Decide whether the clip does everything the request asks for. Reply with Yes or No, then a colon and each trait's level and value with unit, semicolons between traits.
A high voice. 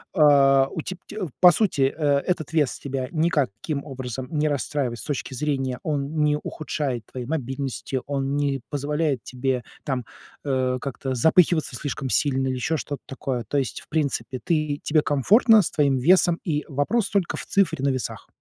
No: medium, 145 Hz